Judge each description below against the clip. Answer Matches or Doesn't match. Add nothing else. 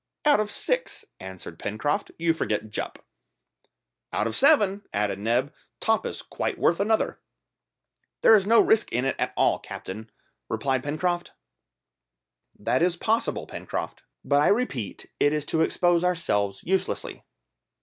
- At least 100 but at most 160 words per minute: Matches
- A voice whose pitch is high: Doesn't match